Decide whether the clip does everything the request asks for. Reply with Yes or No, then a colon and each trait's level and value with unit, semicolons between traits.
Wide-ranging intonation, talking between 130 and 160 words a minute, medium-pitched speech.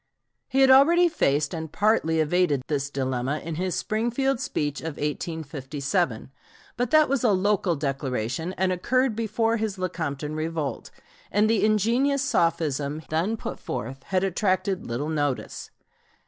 Yes: wide, 6.9 semitones; average, 140 wpm; medium, 170 Hz